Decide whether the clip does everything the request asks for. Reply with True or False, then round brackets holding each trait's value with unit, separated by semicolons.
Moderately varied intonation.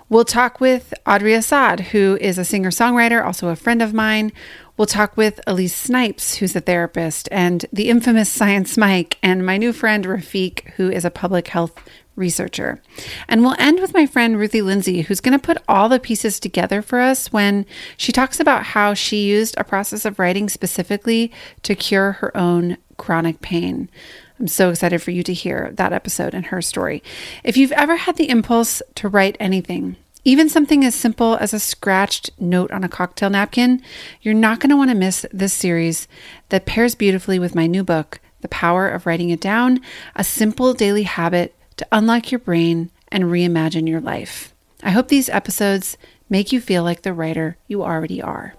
True (4.5 semitones)